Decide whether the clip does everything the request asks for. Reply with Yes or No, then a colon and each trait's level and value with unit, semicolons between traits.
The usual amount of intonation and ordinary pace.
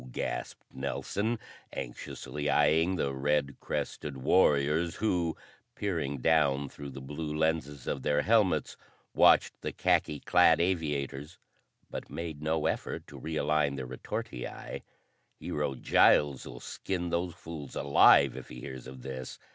No: average, 3.2 semitones; slow, 130 wpm